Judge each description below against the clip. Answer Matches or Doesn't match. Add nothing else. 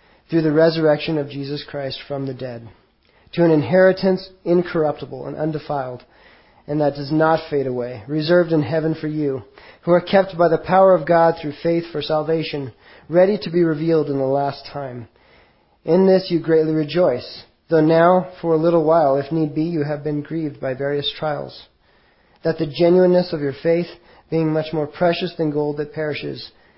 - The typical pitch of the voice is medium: Matches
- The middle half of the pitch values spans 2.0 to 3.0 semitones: Matches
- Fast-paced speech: Doesn't match